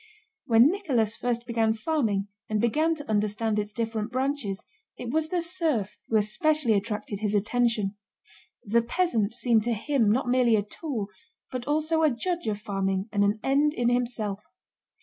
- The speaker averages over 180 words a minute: No, average, 165 wpm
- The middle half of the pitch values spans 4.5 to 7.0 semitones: Yes, average, 5.1 semitones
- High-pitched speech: Yes, high, 235 Hz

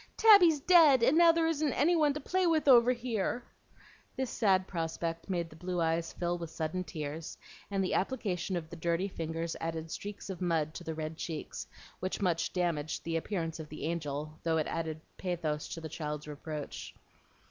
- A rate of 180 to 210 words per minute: Yes, average, 190 wpm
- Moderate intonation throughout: No, wide, 5.9 semitones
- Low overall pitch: No, medium, 170 Hz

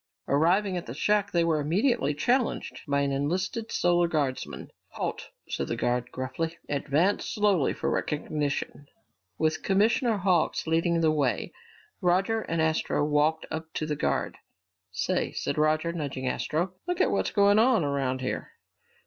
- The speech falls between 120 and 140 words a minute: No, average, 150 wpm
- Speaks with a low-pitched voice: No, medium, 160 Hz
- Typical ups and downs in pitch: Yes, average, 4.9 semitones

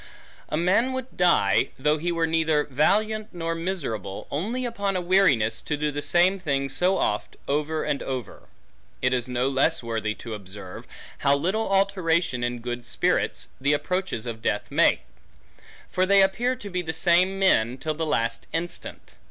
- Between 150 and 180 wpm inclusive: Yes, average, 170 wpm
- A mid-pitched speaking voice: Yes, medium, 160 Hz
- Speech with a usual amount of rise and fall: No, wide, 6.9 semitones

